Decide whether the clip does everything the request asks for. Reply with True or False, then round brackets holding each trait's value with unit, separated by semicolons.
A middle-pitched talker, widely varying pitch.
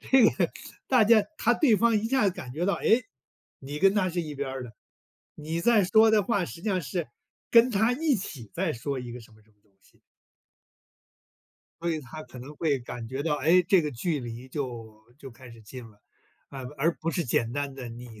True (150 Hz; 7.8 semitones)